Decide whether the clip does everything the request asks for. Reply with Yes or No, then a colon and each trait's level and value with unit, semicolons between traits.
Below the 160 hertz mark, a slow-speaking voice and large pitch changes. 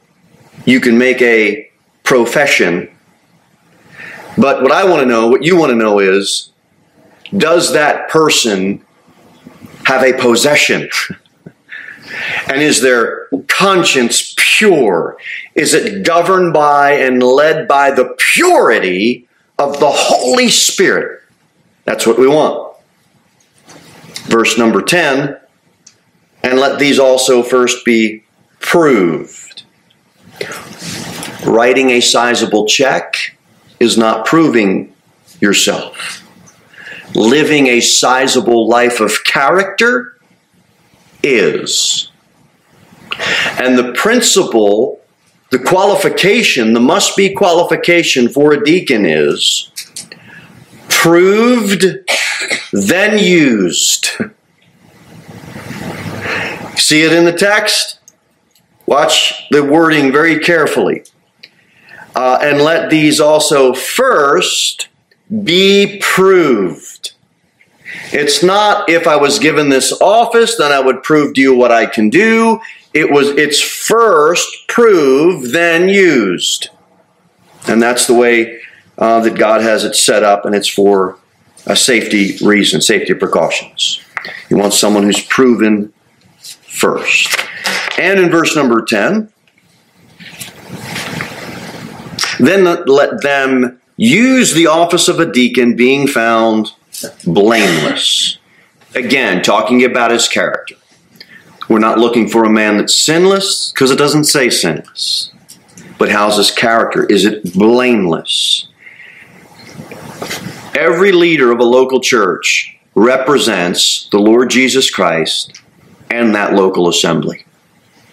Yes: low, 135 Hz; slow, 105 wpm; wide, 7.8 semitones